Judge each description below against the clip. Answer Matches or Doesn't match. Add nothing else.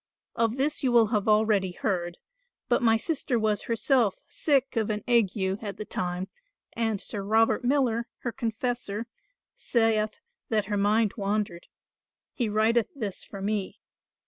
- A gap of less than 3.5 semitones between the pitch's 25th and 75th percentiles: Matches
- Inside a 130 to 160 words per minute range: Matches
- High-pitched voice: Matches